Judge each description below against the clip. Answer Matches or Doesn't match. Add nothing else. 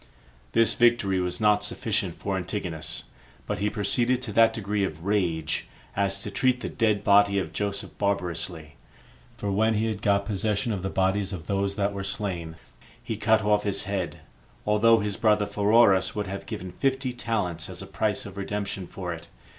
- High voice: Doesn't match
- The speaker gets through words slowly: Doesn't match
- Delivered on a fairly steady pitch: Matches